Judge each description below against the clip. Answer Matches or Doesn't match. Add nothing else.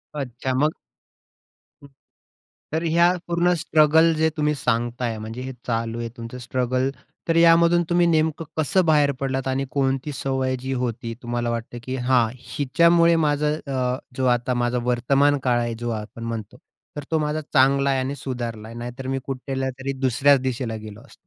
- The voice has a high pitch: Doesn't match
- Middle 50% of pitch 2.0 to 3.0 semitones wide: Doesn't match